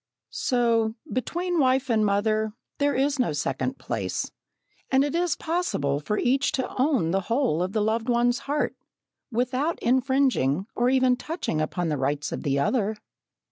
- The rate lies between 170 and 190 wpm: No, average, 160 wpm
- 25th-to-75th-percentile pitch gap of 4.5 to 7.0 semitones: Yes, average, 5.2 semitones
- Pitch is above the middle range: Yes, high, 245 Hz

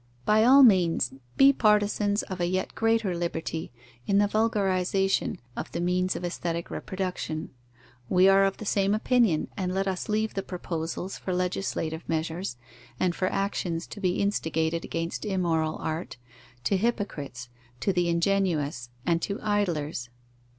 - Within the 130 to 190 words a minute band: Yes, average, 150 wpm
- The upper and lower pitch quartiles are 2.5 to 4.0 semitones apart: Yes, average, 3.3 semitones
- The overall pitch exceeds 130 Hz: Yes, medium, 185 Hz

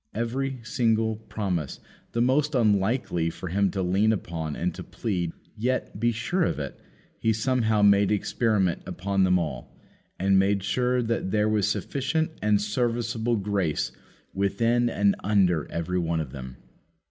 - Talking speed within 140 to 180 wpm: Yes, average, 150 wpm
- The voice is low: Yes, low, 105 Hz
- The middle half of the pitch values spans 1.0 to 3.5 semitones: No, average, 4.0 semitones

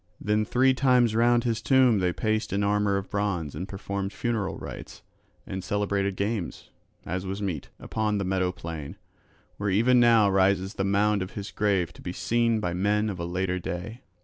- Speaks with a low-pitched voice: Yes, low, 100 Hz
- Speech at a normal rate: Yes, average, 185 wpm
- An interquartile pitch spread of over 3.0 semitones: No, average, 2.7 semitones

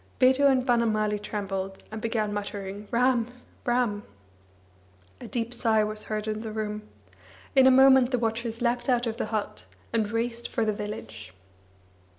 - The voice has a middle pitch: No, high, 225 Hz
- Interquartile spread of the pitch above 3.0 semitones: No, narrow, 2.5 semitones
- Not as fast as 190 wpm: Yes, average, 160 wpm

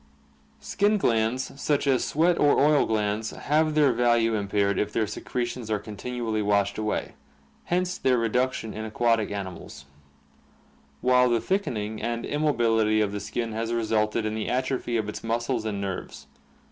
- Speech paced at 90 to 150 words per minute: No, average, 160 wpm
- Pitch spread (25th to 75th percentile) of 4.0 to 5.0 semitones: No, average, 3.1 semitones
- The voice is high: No, low, 115 Hz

